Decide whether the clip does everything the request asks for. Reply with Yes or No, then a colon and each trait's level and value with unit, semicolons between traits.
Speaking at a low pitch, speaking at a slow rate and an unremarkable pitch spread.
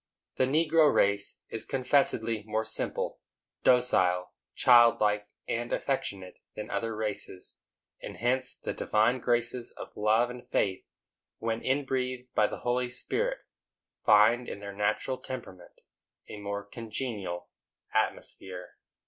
Yes: low, 115 Hz; slow, 125 wpm; average, 3.5 semitones